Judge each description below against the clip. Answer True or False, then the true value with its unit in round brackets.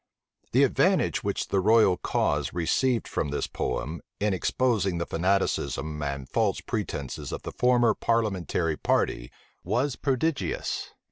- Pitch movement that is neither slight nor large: False (7.2 semitones)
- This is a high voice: False (95 Hz)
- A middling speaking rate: False (130 wpm)